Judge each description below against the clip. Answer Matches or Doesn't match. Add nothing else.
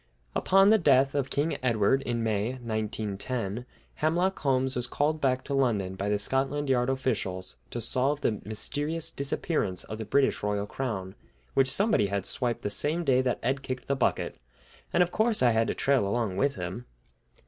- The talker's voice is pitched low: Matches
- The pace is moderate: Matches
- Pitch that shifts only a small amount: Doesn't match